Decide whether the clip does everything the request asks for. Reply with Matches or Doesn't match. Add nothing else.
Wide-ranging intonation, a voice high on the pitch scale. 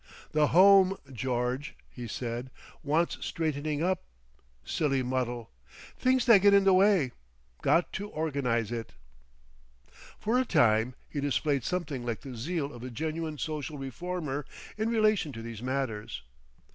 Doesn't match